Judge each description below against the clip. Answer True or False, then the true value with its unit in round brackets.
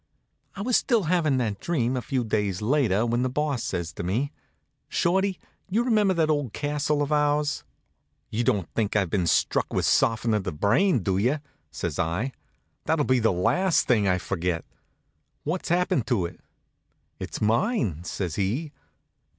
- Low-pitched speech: True (125 Hz)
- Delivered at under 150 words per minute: False (165 wpm)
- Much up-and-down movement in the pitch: True (7.6 semitones)